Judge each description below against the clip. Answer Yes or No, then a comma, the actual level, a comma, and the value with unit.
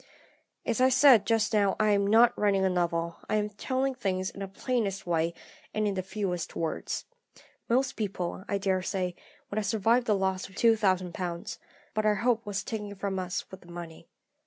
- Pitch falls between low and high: No, high, 200 Hz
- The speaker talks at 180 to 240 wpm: Yes, average, 185 wpm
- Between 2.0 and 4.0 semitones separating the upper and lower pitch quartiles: Yes, average, 2.8 semitones